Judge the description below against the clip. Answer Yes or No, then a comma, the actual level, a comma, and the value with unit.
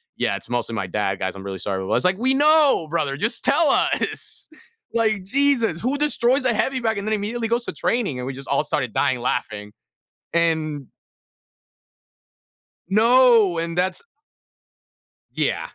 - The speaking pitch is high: Yes, high, 195 Hz